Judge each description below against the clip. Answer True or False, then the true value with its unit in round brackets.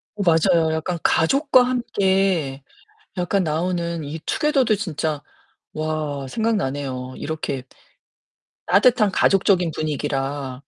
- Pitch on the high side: False (165 Hz)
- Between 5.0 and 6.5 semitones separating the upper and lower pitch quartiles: True (5.3 semitones)